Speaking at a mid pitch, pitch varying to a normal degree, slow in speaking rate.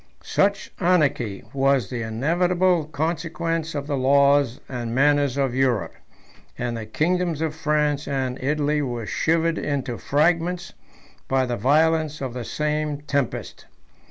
Yes: medium, 145 Hz; average, 3.7 semitones; slow, 130 wpm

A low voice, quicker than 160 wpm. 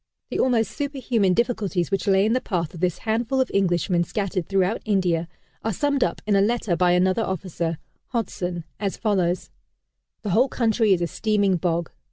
No: high, 195 Hz; average, 180 wpm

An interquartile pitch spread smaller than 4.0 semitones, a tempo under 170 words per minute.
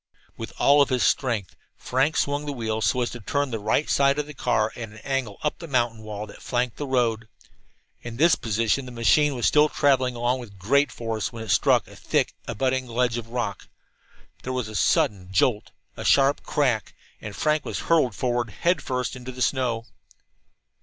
No: average, 3.4 semitones; average, 195 wpm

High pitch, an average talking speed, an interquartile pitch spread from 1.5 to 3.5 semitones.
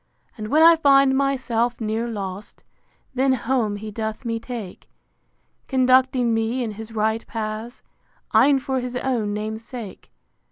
Yes: high, 235 Hz; average, 145 wpm; average, 3.1 semitones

